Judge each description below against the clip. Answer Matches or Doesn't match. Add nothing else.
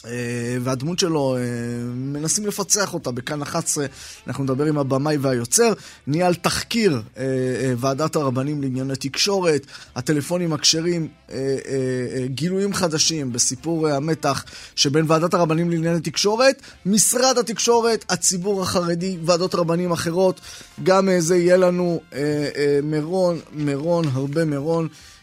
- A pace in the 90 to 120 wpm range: Matches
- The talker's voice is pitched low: Doesn't match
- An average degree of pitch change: Matches